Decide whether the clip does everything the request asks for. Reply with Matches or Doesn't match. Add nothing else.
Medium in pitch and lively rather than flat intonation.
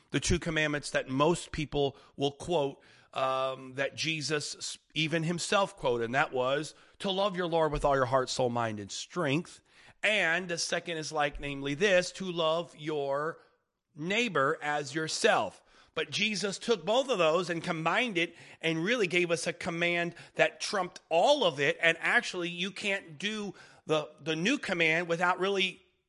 Doesn't match